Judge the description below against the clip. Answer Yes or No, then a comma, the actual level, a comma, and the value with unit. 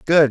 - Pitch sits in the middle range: Yes, medium, 150 Hz